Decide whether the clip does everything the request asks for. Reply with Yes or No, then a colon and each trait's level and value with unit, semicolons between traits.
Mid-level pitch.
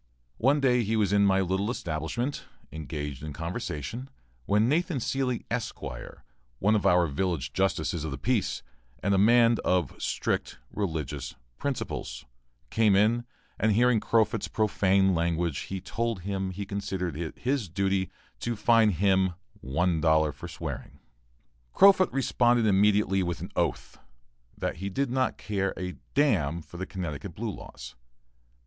No: very low, 95 Hz